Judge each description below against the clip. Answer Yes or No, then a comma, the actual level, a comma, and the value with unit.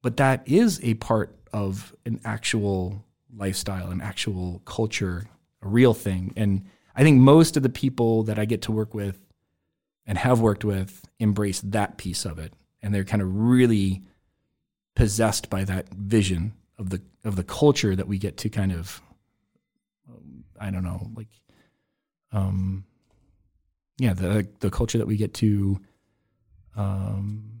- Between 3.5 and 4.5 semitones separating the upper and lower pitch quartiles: No, average, 2.9 semitones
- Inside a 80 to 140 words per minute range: No, average, 155 wpm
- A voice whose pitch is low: Yes, low, 105 Hz